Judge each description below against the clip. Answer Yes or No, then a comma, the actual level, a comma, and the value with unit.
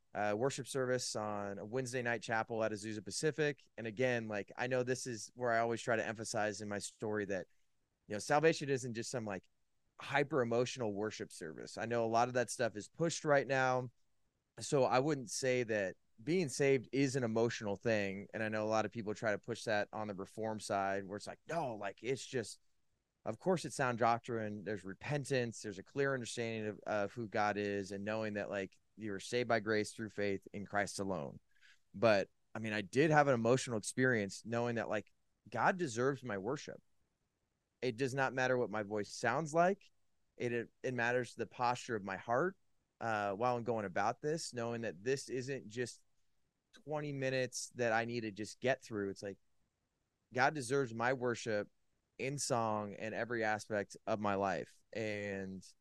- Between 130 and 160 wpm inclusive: No, average, 195 wpm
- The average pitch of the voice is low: Yes, low, 115 Hz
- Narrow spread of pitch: No, average, 3.6 semitones